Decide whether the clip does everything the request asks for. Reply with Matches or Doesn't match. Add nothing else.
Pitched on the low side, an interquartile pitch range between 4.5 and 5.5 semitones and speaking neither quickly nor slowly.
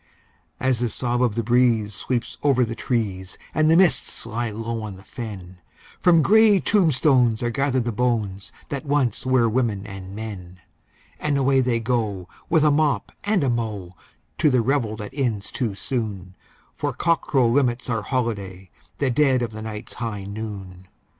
Doesn't match